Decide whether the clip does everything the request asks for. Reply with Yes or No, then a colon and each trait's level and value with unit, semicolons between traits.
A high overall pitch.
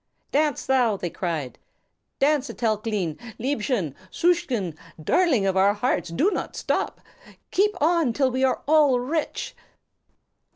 Yes: very high, 250 Hz